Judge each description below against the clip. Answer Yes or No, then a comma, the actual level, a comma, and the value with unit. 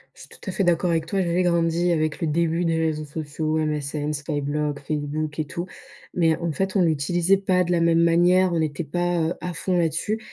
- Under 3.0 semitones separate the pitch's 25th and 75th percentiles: Yes, narrow, 2.4 semitones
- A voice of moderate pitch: Yes, medium, 165 Hz